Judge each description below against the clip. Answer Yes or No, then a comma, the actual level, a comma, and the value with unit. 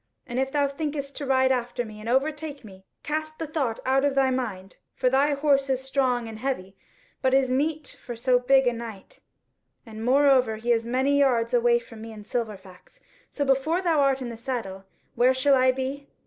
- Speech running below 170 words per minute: No, fast, 205 wpm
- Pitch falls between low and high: No, very high, 260 Hz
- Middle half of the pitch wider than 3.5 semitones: No, average, 3.0 semitones